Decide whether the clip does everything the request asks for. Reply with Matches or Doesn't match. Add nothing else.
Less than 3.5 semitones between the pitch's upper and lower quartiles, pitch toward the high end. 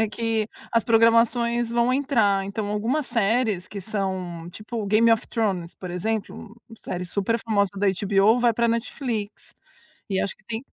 Matches